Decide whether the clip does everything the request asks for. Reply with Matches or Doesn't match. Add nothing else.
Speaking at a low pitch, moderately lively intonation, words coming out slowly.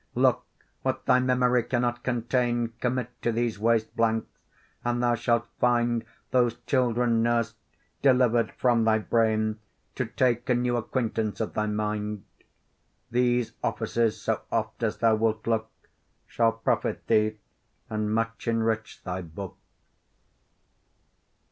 Doesn't match